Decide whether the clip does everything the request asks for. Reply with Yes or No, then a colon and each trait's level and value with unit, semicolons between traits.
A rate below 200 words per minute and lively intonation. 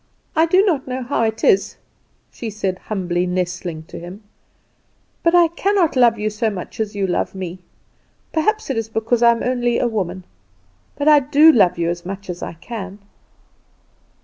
Yes: average, 180 wpm; wide, 6.1 semitones